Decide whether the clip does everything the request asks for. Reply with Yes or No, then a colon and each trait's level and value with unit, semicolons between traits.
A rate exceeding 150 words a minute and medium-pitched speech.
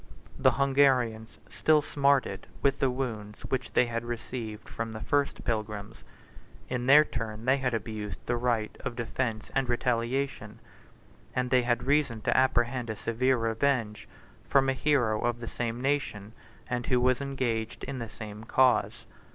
No: average, 160 wpm; low, 120 Hz